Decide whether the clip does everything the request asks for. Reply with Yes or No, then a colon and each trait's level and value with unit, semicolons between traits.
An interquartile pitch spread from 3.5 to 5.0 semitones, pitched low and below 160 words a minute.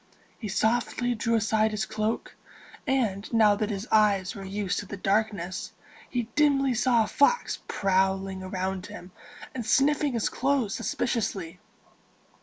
No: average, 3.8 semitones; high, 215 Hz; average, 140 wpm